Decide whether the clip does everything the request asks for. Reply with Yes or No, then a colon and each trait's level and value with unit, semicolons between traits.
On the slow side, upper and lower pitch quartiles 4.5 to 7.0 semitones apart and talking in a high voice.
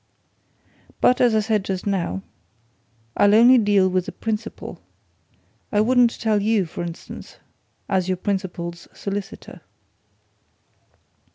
No: slow, 115 wpm; average, 2.9 semitones; high, 205 Hz